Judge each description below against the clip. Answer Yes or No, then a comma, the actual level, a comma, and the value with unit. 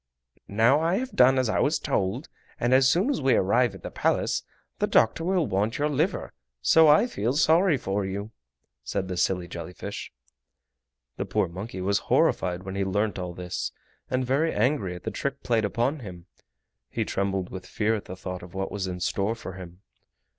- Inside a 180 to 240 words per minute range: Yes, average, 195 wpm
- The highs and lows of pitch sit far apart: Yes, wide, 6.5 semitones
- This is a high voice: No, low, 105 Hz